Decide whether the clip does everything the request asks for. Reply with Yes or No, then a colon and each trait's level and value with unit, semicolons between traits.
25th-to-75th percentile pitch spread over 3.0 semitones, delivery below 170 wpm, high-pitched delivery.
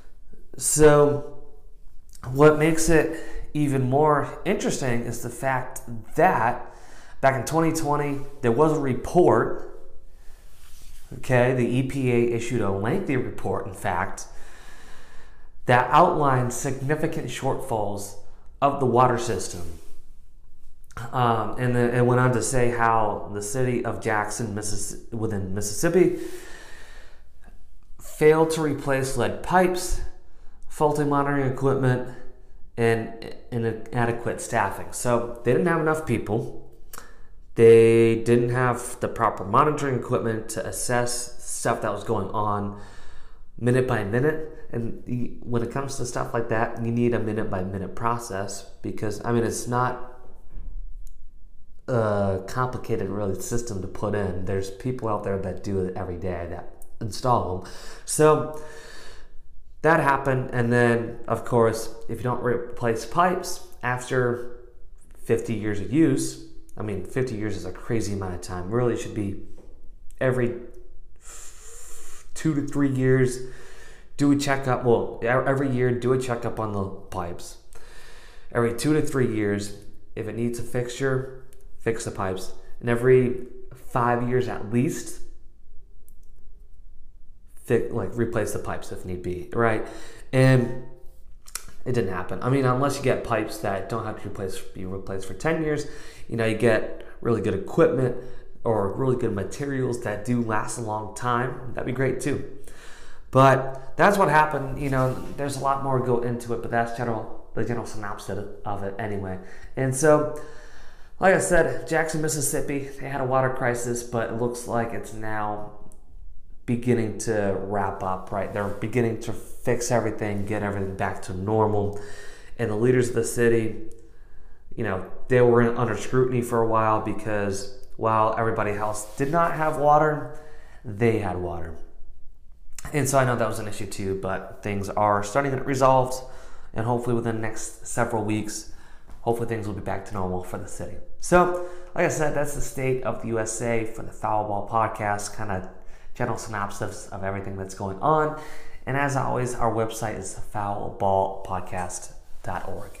No: average, 4.2 semitones; average, 150 wpm; low, 115 Hz